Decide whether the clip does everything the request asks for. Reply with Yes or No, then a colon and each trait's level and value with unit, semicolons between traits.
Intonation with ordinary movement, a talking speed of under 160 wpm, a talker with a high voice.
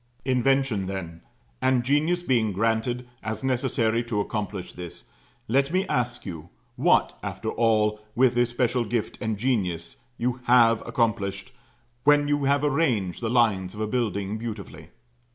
No: average, 3.6 semitones; average, 145 wpm; low, 115 Hz